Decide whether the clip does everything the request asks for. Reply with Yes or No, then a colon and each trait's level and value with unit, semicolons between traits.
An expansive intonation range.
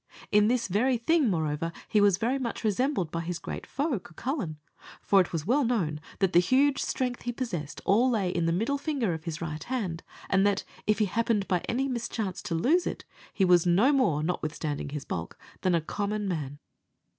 Yes: wide, 6.5 semitones